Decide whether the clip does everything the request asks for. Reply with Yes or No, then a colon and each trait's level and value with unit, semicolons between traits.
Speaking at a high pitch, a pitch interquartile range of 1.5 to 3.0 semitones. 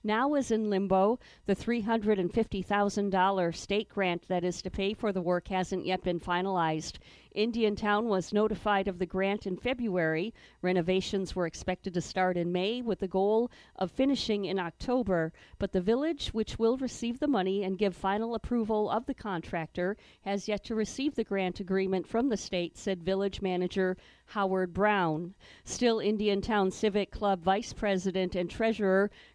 Yes: high, 195 Hz; average, 2.7 semitones